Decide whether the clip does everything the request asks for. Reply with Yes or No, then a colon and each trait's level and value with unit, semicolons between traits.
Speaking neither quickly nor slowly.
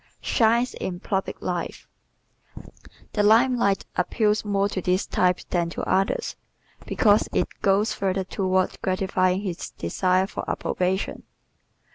No: slow, 130 wpm